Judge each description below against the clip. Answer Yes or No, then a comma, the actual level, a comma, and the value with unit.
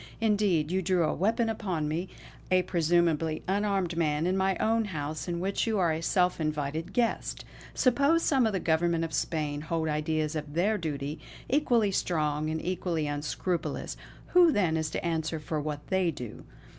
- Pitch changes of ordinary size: Yes, average, 3.8 semitones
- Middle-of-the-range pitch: Yes, medium, 170 Hz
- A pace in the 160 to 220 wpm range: Yes, average, 175 wpm